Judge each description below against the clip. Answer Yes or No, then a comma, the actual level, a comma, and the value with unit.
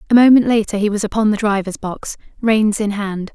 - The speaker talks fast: Yes, fast, 215 wpm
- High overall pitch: Yes, high, 210 Hz